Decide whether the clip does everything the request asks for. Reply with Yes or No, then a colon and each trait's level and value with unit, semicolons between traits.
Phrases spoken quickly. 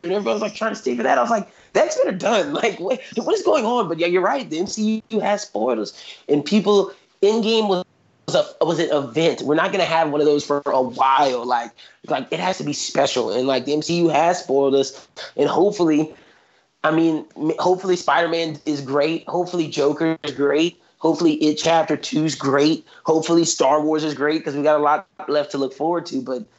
Yes: fast, 215 wpm